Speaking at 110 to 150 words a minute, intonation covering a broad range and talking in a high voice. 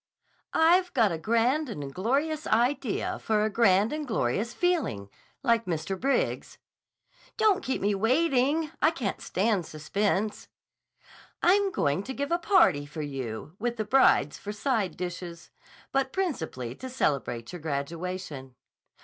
Yes: slow, 135 wpm; wide, 8.7 semitones; high, 215 Hz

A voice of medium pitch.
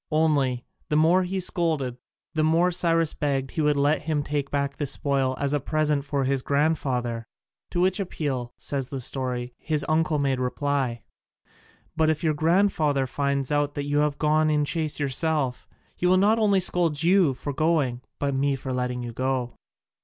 Yes: medium, 145 Hz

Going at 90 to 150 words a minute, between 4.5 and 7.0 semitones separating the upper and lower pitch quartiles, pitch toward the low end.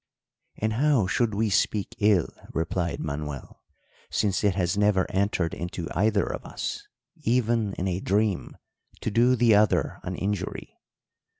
No: average, 140 wpm; average, 3.2 semitones; low, 100 Hz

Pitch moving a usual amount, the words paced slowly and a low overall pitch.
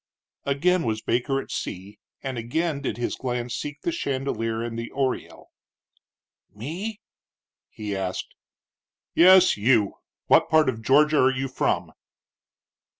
Yes: average, 4.8 semitones; slow, 130 wpm; low, 130 Hz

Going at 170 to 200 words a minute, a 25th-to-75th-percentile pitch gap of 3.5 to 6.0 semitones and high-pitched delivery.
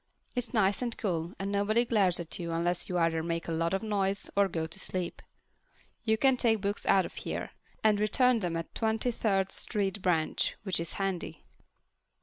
Yes: average, 195 wpm; average, 4.2 semitones; high, 195 Hz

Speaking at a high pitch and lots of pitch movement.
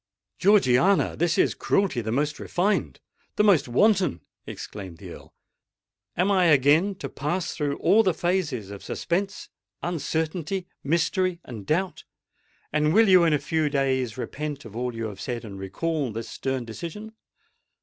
No: medium, 150 Hz; wide, 6.7 semitones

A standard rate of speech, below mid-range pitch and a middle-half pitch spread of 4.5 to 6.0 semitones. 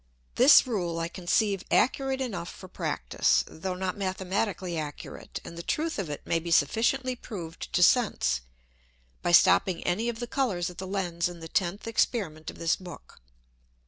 No: average, 170 wpm; medium, 185 Hz; average, 4.9 semitones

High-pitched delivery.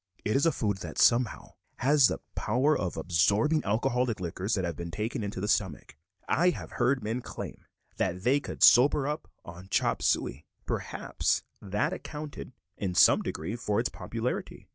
No: low, 110 Hz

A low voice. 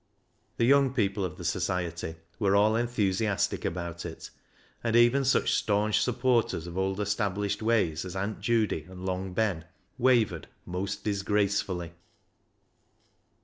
Yes: low, 100 Hz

